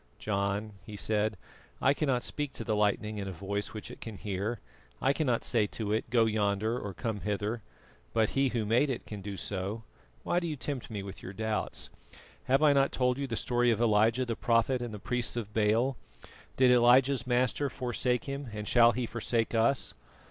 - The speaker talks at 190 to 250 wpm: Yes, average, 200 wpm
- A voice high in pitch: No, low, 115 Hz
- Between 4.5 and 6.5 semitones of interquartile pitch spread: No, average, 3.2 semitones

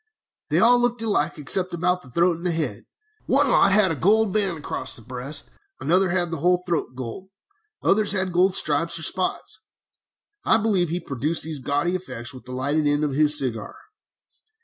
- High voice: No, medium, 170 Hz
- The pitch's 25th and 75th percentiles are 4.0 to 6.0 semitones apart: Yes, average, 4.4 semitones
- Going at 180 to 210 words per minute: Yes, average, 185 wpm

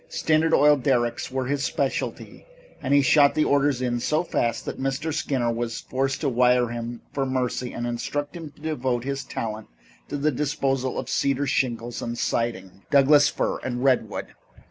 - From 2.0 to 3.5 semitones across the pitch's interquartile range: Yes, average, 3.1 semitones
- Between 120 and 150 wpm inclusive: No, average, 175 wpm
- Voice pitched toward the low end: Yes, low, 130 Hz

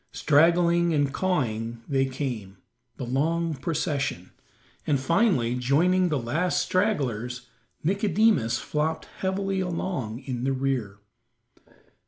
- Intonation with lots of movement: Yes, wide, 5.9 semitones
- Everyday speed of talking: No, slow, 105 wpm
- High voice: No, medium, 145 Hz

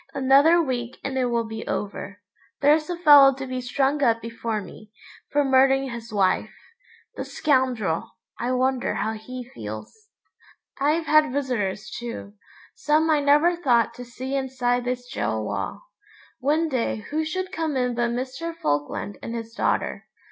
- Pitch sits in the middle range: No, very high, 255 Hz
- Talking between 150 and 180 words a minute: Yes, average, 155 wpm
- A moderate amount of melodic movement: Yes, average, 4.0 semitones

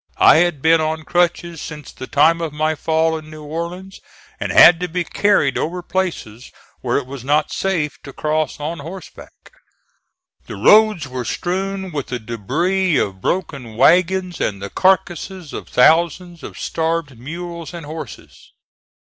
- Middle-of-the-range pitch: Yes, medium, 160 Hz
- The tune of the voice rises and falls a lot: No, average, 3.3 semitones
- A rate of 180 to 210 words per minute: No, average, 160 wpm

